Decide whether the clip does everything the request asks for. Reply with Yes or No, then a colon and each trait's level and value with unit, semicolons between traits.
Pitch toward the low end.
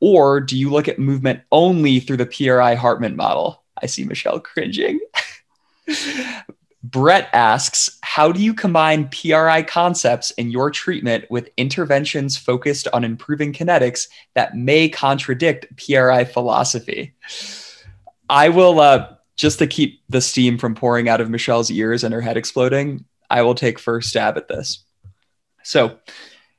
Yes: low, 130 Hz